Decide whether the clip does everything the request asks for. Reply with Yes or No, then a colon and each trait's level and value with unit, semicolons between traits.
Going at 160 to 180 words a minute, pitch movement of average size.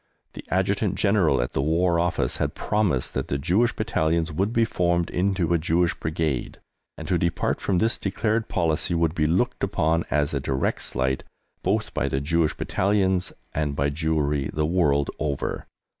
Yes: average, 175 wpm; average, 3.8 semitones